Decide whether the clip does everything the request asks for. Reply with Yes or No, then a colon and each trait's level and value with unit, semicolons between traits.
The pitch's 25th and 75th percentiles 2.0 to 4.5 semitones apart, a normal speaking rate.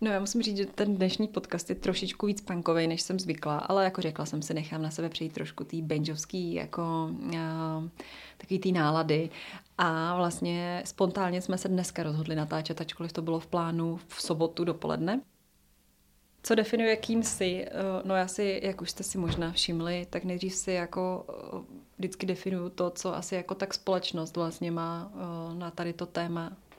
No: narrow, 2.4 semitones; fast, 175 wpm